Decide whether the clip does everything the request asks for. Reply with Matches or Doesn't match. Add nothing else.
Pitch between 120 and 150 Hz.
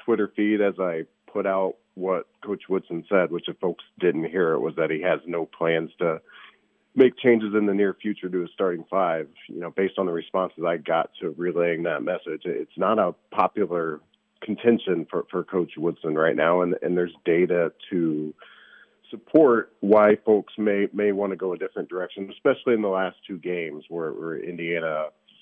Doesn't match